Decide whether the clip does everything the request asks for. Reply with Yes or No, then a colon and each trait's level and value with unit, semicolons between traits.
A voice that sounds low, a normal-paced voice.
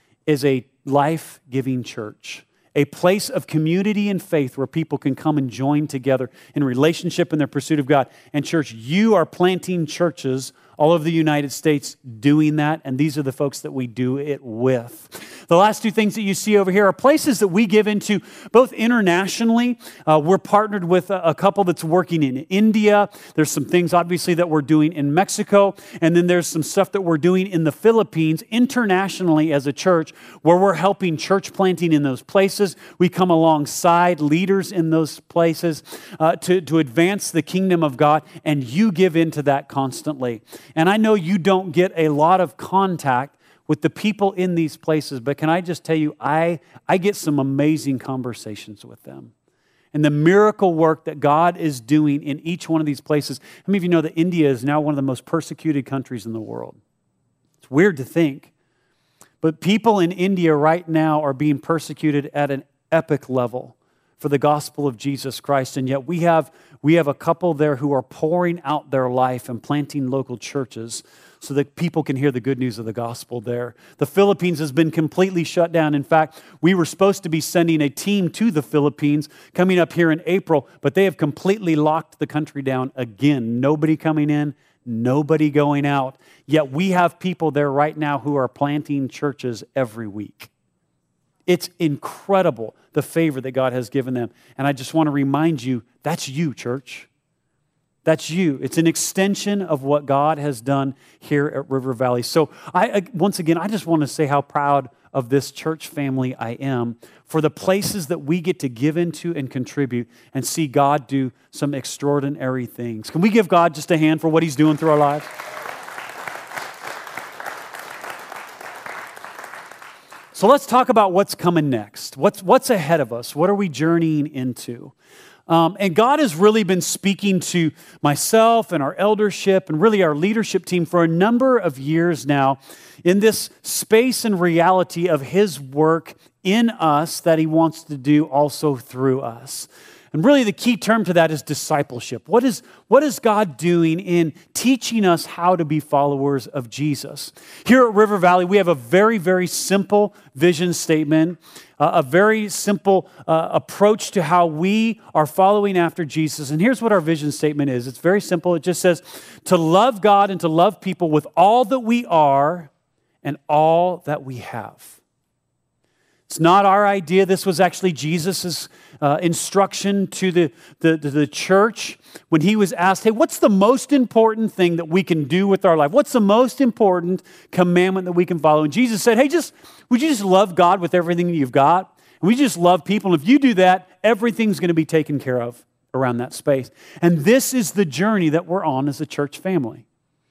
No: medium, 160 Hz; average, 190 wpm